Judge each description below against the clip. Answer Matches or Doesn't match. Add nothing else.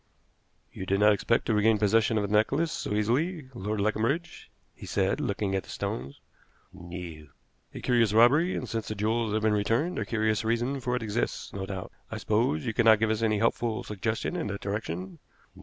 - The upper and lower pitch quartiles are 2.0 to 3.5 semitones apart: Matches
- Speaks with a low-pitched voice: Matches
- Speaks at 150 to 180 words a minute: Doesn't match